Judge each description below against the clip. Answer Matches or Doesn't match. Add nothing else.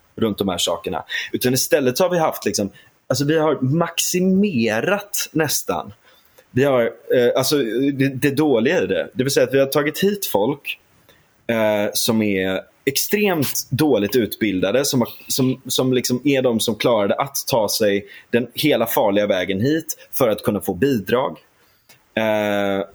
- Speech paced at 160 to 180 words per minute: Matches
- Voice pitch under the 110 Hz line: Doesn't match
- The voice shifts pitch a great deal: Matches